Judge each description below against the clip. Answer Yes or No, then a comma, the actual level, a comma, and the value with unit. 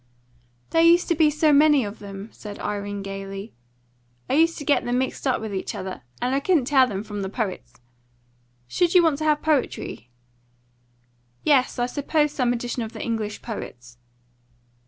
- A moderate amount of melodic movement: No, wide, 6.6 semitones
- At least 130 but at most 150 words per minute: No, average, 175 wpm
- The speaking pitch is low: No, high, 245 Hz